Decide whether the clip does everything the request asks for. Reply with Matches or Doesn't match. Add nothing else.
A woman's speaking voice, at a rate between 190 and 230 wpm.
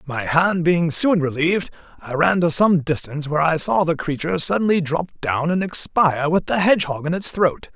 Doesn't match